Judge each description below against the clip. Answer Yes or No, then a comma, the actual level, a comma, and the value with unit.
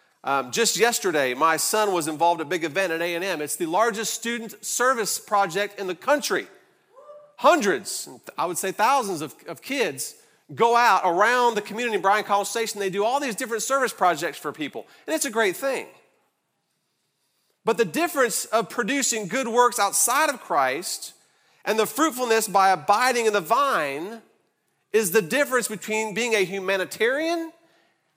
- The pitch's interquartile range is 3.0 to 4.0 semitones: No, average, 4.7 semitones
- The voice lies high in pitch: Yes, high, 225 Hz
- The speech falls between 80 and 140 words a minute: No, average, 175 wpm